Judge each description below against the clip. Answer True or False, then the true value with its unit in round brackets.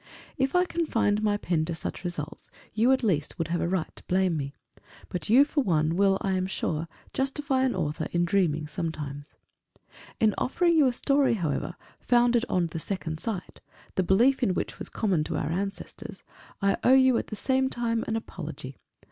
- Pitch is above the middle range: True (195 Hz)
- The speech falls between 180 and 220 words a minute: True (190 wpm)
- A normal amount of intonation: False (6.9 semitones)